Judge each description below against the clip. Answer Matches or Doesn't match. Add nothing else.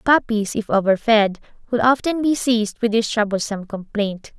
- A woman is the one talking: Matches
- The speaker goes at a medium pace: Matches